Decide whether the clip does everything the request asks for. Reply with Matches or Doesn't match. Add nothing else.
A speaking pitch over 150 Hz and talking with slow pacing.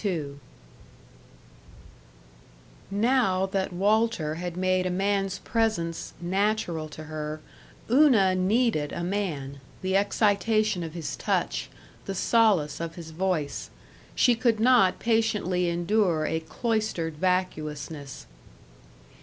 Matches